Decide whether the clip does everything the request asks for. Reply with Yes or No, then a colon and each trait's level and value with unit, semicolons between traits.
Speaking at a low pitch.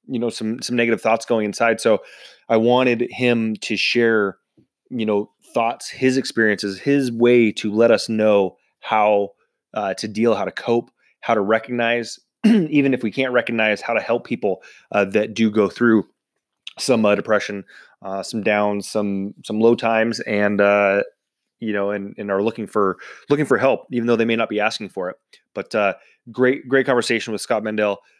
Yes: low, 115 Hz